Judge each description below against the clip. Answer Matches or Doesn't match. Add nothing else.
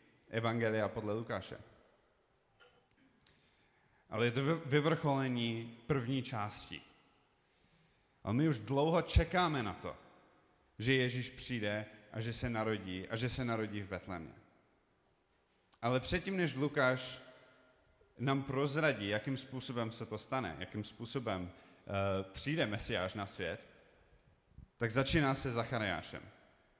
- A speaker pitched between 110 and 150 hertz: Matches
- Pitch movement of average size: Matches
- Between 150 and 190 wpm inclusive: Doesn't match